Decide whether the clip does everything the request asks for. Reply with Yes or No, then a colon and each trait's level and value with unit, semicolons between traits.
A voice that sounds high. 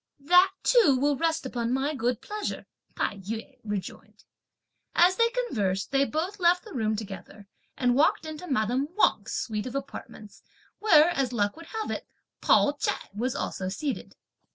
Yes: very high, 270 Hz